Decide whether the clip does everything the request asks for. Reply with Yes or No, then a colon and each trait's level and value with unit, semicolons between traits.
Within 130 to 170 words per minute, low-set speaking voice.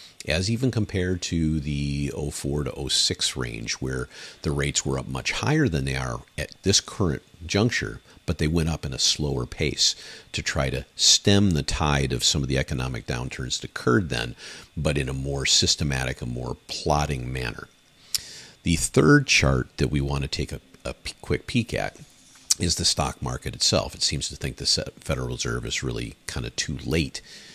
No: average, 185 wpm; very low, 70 Hz